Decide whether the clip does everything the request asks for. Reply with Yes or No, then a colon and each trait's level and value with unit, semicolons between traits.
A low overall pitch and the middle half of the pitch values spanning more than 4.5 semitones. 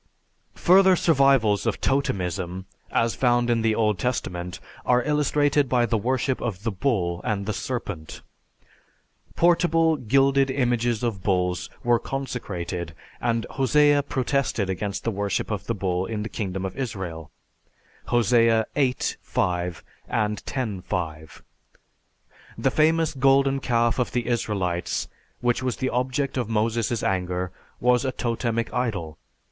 Yes: low, 115 Hz; wide, 5.4 semitones